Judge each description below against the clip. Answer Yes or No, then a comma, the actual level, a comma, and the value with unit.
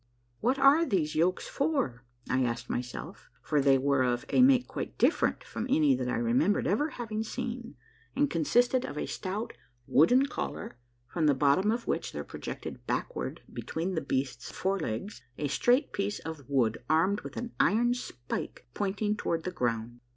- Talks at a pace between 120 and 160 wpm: No, average, 175 wpm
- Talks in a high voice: No, medium, 165 Hz